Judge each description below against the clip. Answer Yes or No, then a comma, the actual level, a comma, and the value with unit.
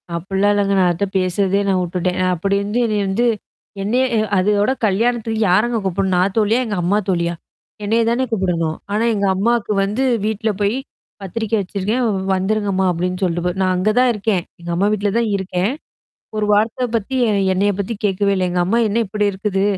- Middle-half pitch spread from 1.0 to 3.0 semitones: Yes, average, 2.7 semitones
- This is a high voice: Yes, high, 200 Hz